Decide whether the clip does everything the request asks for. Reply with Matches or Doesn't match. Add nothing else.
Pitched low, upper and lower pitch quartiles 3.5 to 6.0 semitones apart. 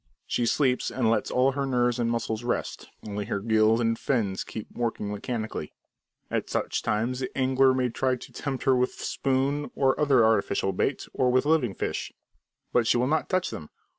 Doesn't match